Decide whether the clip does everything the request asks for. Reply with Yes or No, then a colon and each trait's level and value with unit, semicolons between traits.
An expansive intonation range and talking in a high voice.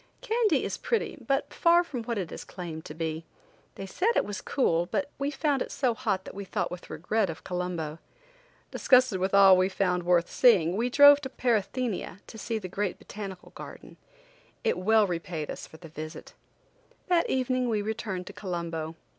Yes: wide, 6.3 semitones; high, 200 Hz